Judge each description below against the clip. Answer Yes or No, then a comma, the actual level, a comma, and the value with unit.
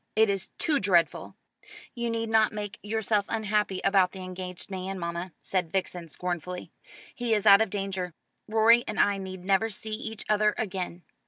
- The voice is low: No, high, 195 Hz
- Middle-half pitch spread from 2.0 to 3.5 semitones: Yes, average, 2.9 semitones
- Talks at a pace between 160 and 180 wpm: Yes, average, 170 wpm